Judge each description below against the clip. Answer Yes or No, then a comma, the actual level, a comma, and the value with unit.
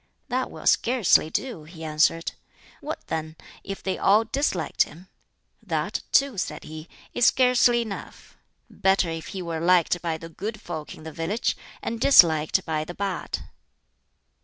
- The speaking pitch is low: No, medium, 180 Hz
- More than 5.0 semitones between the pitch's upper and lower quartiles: Yes, wide, 5.5 semitones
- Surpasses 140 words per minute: Yes, average, 155 wpm